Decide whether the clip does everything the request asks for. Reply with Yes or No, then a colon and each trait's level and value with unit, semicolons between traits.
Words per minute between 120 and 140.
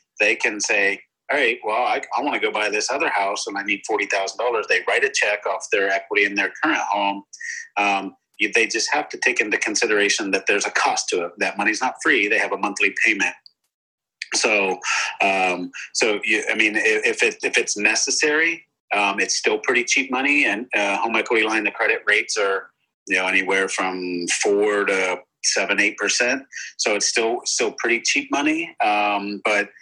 No: average, 200 wpm